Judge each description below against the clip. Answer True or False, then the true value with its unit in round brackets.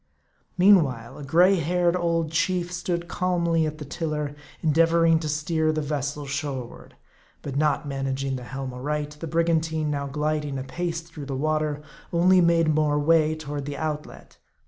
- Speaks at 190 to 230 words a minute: False (155 wpm)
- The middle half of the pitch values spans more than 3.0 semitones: False (2.5 semitones)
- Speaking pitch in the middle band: True (155 Hz)